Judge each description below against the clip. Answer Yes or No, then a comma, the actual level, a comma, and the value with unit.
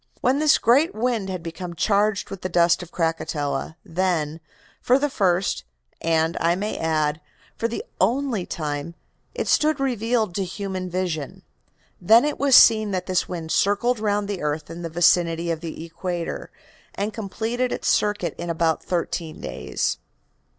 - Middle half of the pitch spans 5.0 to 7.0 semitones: No, average, 4.6 semitones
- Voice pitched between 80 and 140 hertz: No, medium, 185 Hz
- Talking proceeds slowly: No, average, 160 wpm